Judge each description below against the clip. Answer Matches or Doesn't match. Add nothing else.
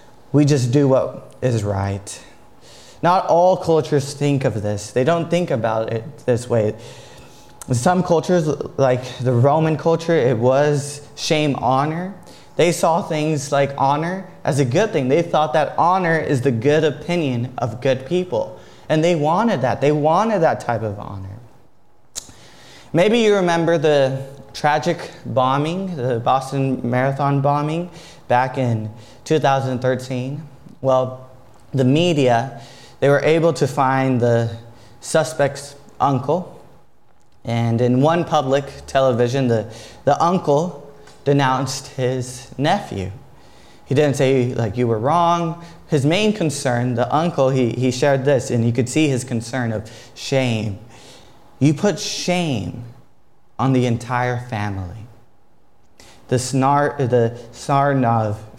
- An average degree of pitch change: Matches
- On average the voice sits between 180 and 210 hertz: Doesn't match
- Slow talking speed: Matches